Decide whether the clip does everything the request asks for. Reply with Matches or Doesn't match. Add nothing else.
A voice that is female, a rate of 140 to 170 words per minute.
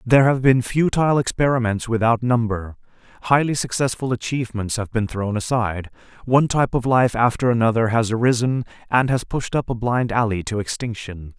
Doesn't match